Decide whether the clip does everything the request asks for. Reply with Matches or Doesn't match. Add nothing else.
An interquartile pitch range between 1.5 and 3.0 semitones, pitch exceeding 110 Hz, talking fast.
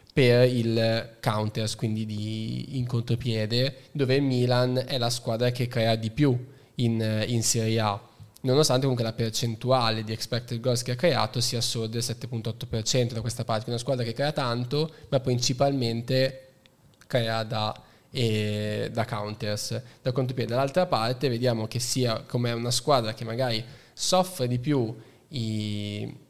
Doesn't match